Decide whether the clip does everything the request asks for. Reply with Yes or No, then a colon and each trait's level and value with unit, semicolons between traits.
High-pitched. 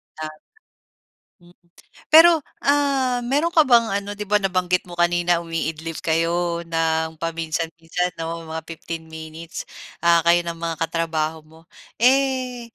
No: medium, 170 Hz